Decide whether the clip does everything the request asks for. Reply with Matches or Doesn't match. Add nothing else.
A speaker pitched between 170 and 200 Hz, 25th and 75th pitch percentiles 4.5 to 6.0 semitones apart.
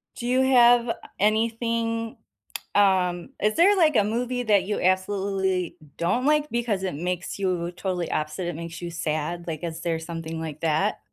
Matches